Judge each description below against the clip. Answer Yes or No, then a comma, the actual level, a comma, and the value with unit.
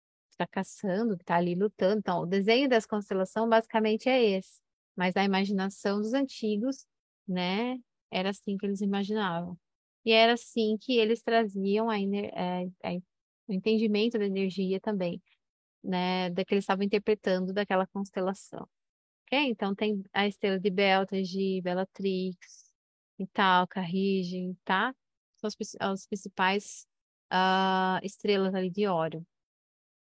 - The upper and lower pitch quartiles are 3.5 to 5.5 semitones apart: No, narrow, 2.4 semitones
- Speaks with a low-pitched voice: No, high, 195 Hz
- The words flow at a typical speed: Yes, average, 130 wpm